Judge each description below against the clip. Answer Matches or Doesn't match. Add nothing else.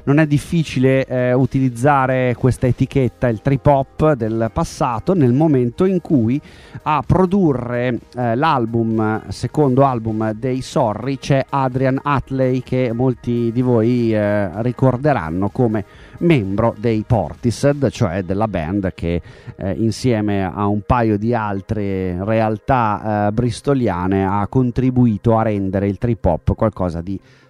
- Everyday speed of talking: Matches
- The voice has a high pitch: Doesn't match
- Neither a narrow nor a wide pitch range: Matches